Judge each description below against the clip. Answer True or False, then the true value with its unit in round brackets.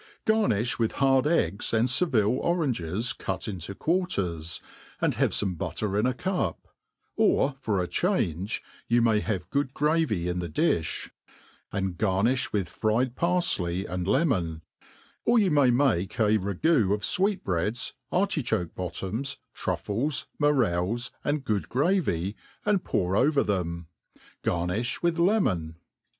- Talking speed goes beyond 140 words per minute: False (135 wpm)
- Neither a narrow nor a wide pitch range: False (8.0 semitones)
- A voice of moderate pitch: False (110 Hz)